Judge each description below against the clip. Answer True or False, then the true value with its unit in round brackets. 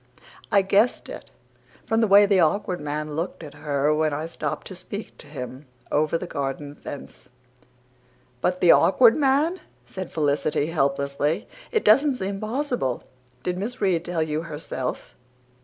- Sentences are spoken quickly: False (155 wpm)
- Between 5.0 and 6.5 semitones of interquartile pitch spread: True (5.5 semitones)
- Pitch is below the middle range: False (165 Hz)